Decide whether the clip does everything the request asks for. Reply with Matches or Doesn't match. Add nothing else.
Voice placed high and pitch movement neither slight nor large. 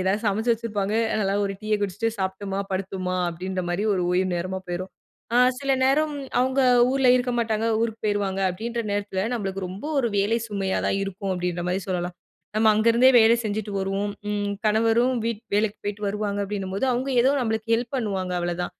Matches